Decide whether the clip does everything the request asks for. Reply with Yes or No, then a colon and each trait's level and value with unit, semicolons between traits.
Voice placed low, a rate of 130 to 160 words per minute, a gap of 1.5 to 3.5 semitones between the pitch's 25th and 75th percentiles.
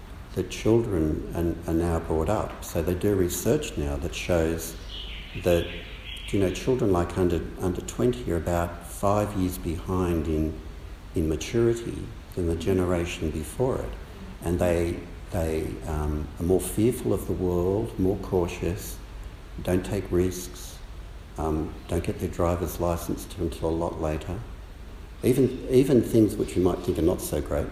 Yes: very low, 90 Hz; average, 155 wpm; average, 2.7 semitones